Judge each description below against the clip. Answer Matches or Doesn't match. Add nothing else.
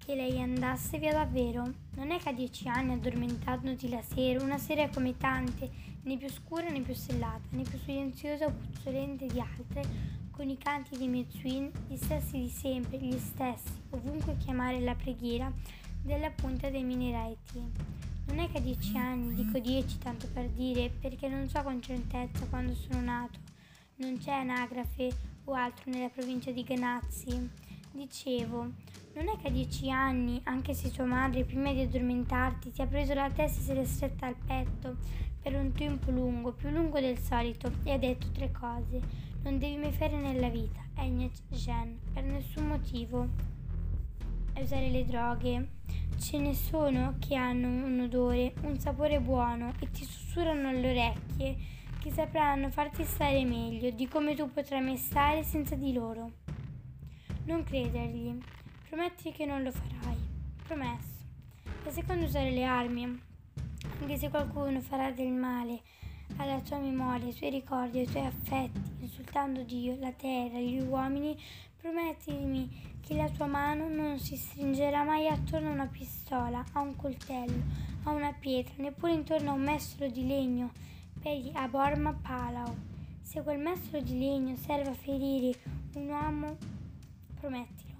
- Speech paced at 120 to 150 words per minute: Doesn't match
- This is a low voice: Doesn't match